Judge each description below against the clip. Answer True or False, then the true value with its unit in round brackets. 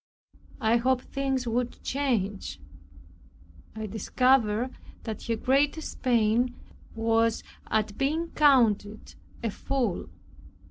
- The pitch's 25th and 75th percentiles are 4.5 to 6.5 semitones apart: False (3.4 semitones)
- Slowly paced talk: True (95 wpm)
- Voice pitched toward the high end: True (235 Hz)